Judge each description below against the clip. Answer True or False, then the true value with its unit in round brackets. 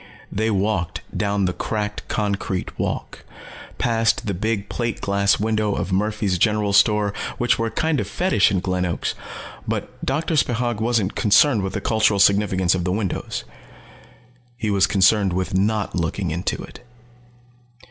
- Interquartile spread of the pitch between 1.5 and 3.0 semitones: True (2.5 semitones)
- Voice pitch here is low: True (105 Hz)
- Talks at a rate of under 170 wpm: True (155 wpm)